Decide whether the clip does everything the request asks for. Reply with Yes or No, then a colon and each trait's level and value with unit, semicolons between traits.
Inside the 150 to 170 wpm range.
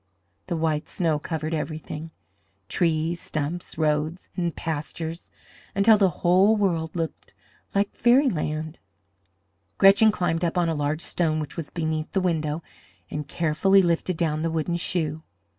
No: average, 140 wpm